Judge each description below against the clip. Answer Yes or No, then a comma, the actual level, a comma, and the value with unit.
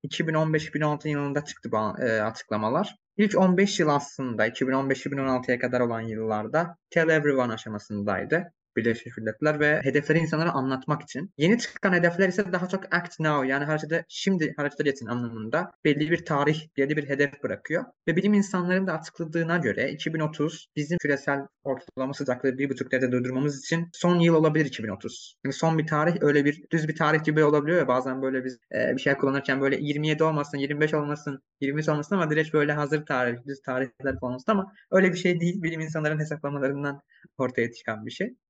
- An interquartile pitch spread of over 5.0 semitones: No, average, 3.4 semitones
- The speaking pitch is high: No, medium, 150 Hz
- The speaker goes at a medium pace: No, fast, 175 wpm